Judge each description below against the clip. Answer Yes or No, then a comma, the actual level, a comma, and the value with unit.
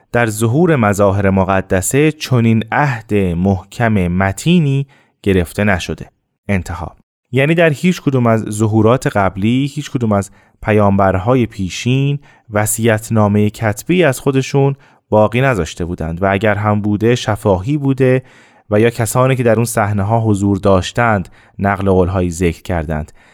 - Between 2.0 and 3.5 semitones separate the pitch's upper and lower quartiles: No, average, 4.8 semitones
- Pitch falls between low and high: No, low, 110 Hz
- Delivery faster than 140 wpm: No, average, 135 wpm